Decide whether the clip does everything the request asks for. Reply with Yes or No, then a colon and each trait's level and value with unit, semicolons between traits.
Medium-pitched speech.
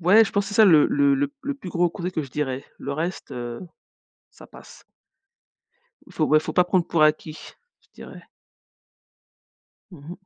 Yes: medium, 175 Hz